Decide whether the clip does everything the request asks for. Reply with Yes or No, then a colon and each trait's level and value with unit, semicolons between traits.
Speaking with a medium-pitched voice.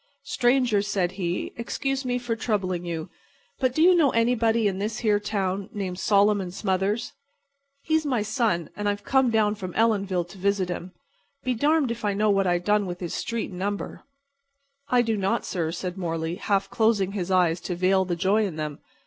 No: high, 200 Hz